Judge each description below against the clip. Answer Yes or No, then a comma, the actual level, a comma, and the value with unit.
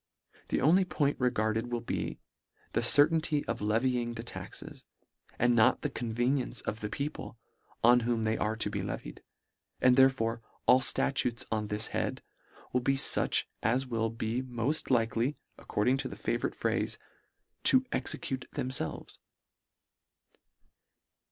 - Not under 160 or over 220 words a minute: No, average, 140 wpm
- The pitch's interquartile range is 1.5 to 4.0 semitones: Yes, average, 2.8 semitones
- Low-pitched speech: Yes, low, 120 Hz